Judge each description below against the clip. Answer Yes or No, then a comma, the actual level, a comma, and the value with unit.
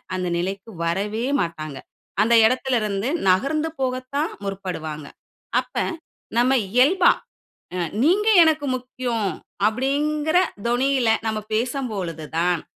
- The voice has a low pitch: No, high, 235 Hz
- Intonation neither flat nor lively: No, wide, 6.2 semitones